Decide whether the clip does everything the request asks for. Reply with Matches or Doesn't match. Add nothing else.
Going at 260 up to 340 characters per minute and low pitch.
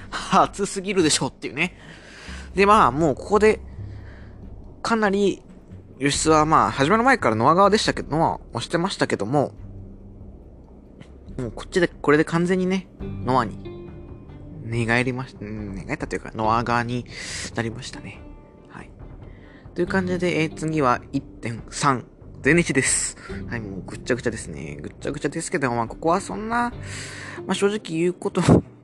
Matches